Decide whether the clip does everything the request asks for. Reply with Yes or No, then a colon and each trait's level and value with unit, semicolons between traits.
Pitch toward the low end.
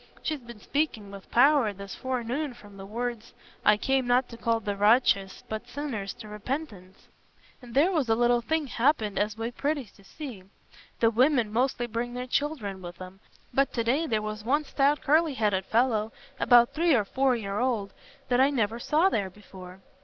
No: high, 235 Hz